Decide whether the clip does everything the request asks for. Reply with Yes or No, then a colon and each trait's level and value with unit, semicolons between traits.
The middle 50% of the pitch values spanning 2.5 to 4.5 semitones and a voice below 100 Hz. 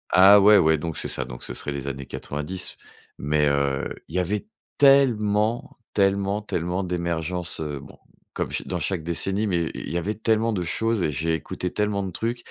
No: average, 4.9 semitones; very low, 90 Hz